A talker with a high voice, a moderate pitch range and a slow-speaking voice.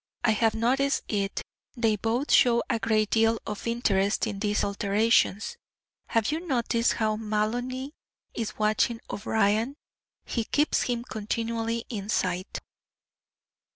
No: high, 225 Hz; narrow, 1.9 semitones; slow, 125 wpm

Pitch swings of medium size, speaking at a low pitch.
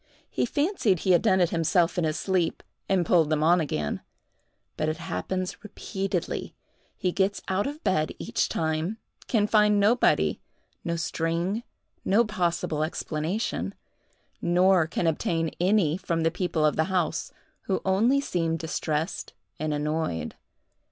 No: average, 3.4 semitones; medium, 175 Hz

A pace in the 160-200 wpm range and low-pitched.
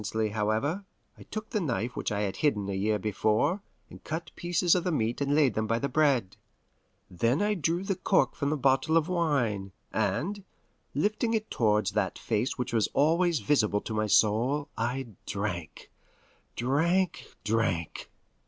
Yes: average, 170 wpm; low, 130 Hz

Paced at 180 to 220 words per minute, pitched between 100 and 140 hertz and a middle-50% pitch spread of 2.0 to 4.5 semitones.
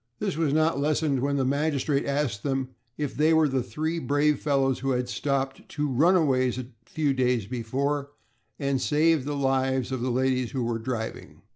Yes: average, 185 wpm; low, 135 Hz; narrow, 2.4 semitones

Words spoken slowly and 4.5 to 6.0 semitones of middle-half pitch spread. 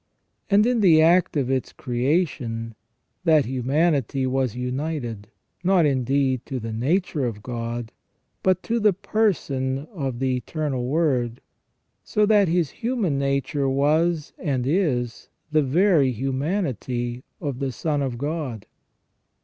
Yes: slow, 130 wpm; average, 4.9 semitones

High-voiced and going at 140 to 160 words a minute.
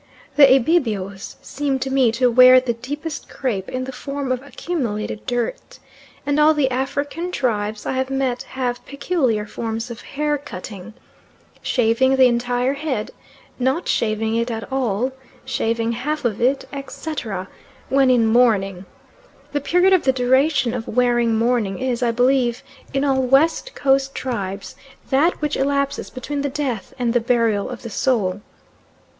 Yes: very high, 255 Hz; average, 155 wpm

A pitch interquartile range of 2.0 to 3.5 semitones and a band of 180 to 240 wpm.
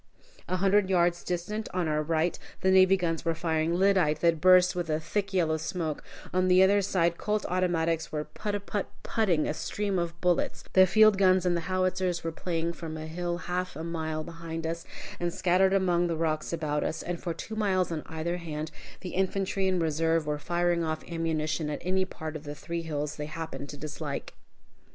Yes: narrow, 2.6 semitones; average, 200 wpm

